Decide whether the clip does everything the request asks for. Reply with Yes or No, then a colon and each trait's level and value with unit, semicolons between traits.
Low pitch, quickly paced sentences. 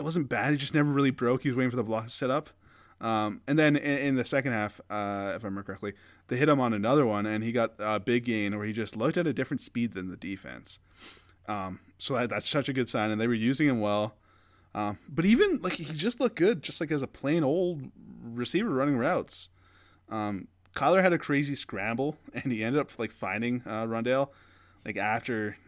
Yes: low, 120 Hz; fast, 235 wpm